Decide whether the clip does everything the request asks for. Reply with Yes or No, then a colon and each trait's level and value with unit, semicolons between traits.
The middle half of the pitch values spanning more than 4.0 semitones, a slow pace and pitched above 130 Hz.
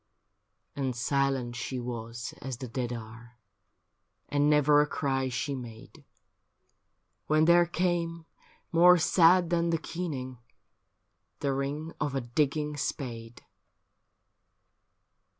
Yes: average, 4.7 semitones; slow, 110 wpm; medium, 140 Hz